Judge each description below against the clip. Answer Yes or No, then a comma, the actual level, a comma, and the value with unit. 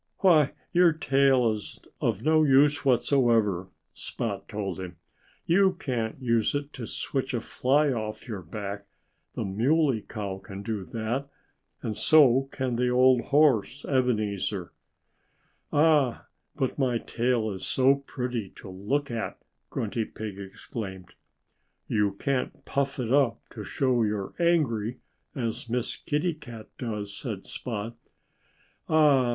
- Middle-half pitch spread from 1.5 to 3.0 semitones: No, average, 4.6 semitones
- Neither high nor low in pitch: No, low, 120 Hz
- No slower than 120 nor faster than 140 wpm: Yes, slow, 135 wpm